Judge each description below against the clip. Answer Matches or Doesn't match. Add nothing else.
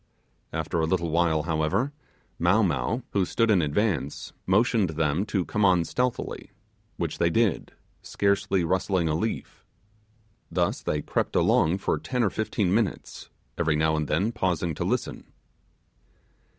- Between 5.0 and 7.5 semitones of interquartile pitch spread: Doesn't match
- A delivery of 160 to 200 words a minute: Doesn't match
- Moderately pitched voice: Doesn't match